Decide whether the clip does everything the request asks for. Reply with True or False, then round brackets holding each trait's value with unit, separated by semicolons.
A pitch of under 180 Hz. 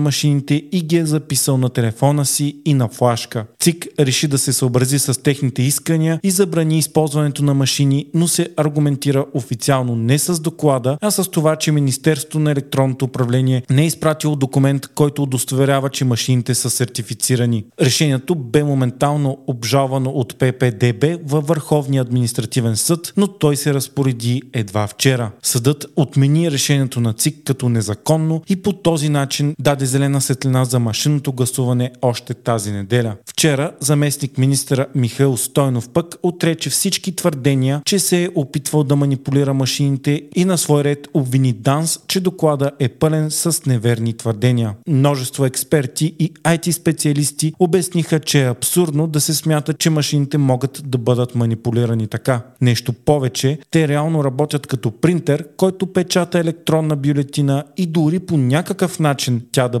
True (140 Hz)